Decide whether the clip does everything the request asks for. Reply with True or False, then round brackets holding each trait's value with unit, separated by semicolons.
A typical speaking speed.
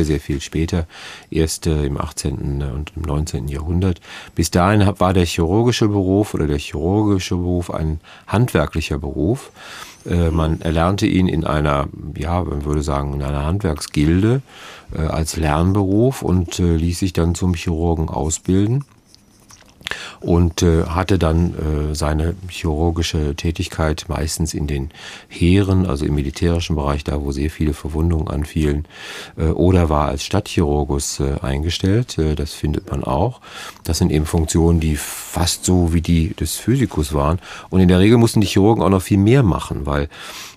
True (150 wpm)